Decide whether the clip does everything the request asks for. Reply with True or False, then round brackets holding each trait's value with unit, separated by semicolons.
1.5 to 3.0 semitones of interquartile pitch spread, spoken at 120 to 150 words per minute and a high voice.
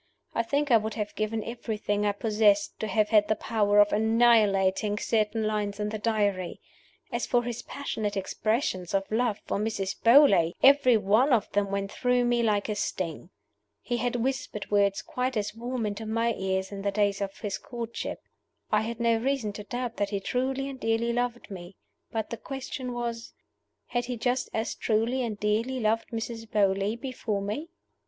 False (2.7 semitones; 185 wpm; 220 Hz)